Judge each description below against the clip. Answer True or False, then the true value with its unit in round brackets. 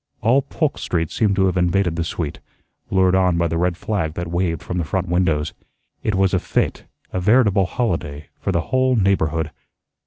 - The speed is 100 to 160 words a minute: False (190 wpm)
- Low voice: True (90 Hz)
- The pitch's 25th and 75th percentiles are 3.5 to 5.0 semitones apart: False (2.8 semitones)